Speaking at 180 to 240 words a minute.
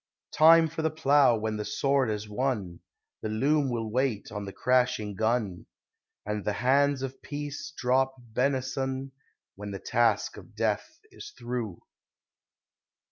No: average, 140 wpm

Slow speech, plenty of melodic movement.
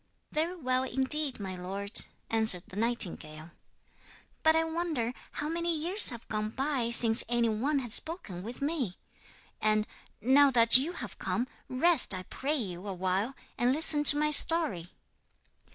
No: average, 150 wpm; wide, 6.2 semitones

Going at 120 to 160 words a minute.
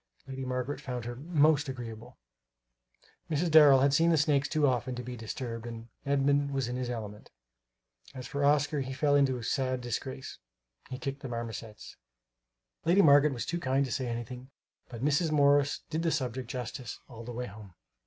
No: average, 180 wpm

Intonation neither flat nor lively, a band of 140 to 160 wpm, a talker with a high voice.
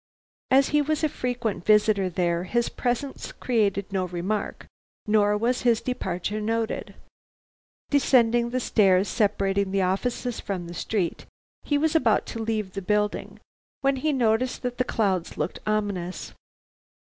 Yes: average, 4.2 semitones; average, 145 wpm; high, 215 Hz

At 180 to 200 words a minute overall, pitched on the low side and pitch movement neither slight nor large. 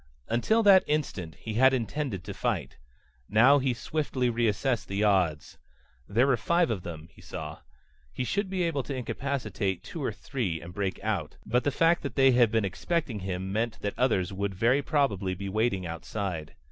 No: average, 185 wpm; low, 115 Hz; wide, 6.1 semitones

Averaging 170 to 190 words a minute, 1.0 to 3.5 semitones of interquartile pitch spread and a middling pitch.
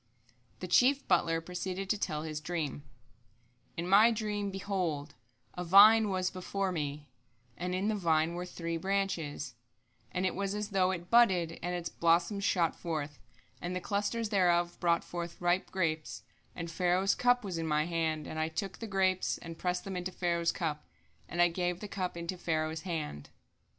Yes: average, 175 wpm; average, 2.8 semitones; medium, 175 Hz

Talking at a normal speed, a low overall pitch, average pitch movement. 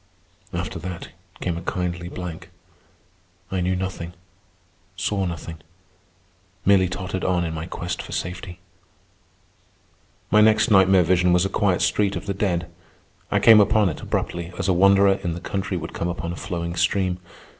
No: average, 160 wpm; very low, 90 Hz; narrow, 2.0 semitones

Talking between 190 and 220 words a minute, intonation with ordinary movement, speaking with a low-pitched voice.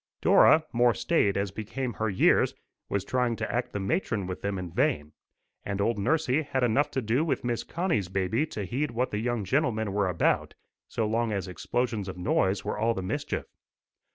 Yes: average, 195 wpm; average, 4.3 semitones; low, 110 Hz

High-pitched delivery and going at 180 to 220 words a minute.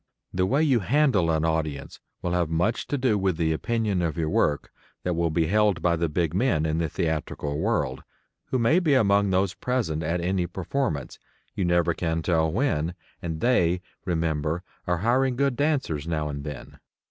No: very low, 85 Hz; average, 185 wpm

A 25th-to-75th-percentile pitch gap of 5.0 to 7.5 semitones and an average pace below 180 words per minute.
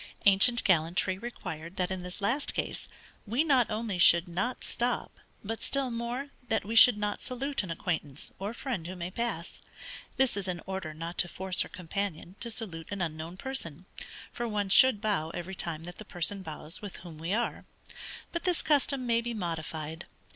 No: wide, 5.5 semitones; average, 185 wpm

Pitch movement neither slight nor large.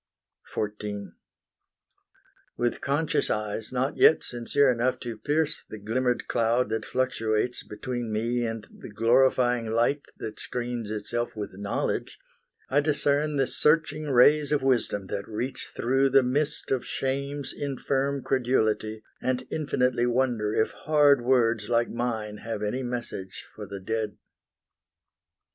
Yes: average, 3.6 semitones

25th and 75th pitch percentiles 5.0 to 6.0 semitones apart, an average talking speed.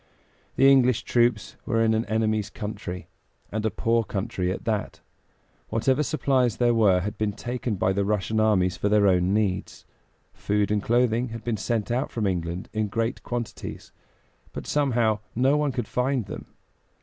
No: average, 2.9 semitones; average, 170 wpm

